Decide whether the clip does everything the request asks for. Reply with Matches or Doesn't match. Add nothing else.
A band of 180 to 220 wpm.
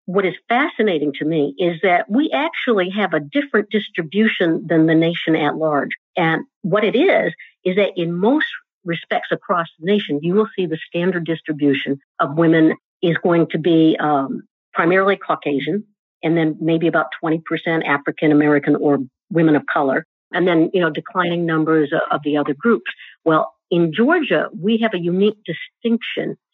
Doesn't match